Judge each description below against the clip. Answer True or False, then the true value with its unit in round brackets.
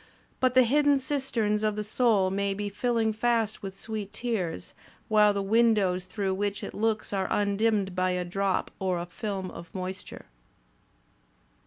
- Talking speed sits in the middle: True (165 wpm)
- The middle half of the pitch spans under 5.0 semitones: True (2.9 semitones)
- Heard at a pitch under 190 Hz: False (205 Hz)